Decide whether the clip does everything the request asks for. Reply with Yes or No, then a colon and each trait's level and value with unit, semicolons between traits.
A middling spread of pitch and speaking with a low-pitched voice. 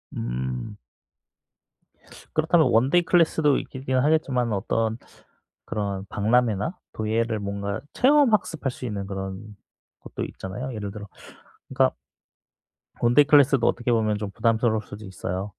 Yes: average, 4.8 semitones; low, 115 Hz